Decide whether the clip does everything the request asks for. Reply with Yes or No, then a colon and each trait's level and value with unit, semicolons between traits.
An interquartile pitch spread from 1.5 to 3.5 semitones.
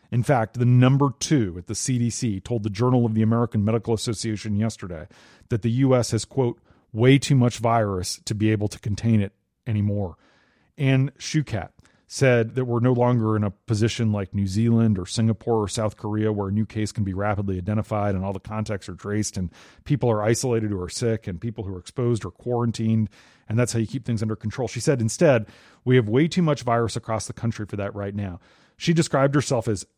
Yes: average, 2.8 semitones